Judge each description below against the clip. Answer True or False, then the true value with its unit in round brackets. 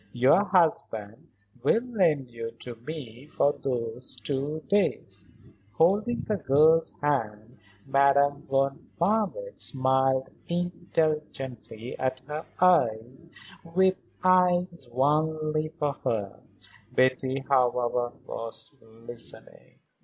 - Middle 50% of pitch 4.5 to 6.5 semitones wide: True (5.1 semitones)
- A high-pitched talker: False (140 Hz)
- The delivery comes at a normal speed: False (95 wpm)